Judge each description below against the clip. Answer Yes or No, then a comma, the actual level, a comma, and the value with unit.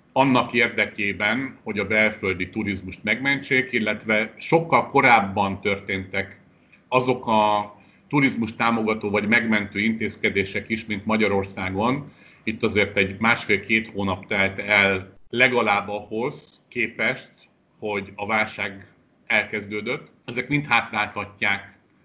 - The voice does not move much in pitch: Yes, narrow, 2.2 semitones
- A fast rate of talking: No, slow, 105 wpm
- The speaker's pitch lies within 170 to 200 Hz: No, low, 105 Hz